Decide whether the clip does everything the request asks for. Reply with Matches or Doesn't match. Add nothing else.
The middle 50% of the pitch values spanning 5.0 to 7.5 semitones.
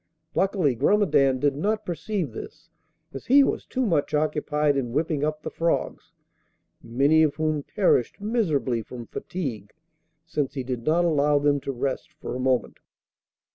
Doesn't match